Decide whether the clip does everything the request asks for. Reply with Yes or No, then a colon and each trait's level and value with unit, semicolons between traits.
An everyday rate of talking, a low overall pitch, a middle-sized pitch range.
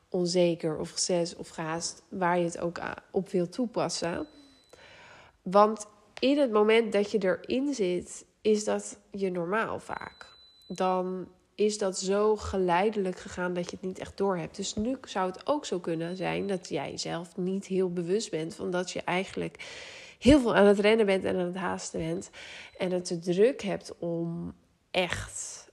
No: average, 175 wpm; high, 190 Hz; average, 3.3 semitones